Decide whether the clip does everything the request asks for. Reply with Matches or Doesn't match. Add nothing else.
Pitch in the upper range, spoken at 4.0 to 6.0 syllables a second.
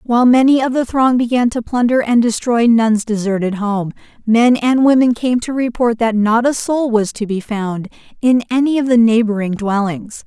Matches